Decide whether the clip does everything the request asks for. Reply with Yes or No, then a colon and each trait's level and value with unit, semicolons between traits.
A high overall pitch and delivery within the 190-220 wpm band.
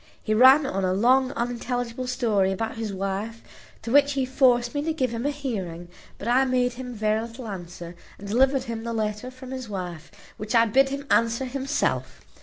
Yes: high, 235 Hz; average, 200 wpm